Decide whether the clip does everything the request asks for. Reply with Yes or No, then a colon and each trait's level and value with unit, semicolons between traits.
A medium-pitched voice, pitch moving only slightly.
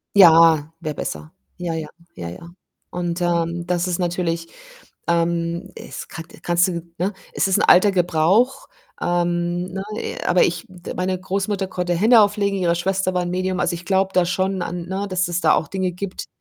Yes: medium, 175 Hz; narrow, 1.8 semitones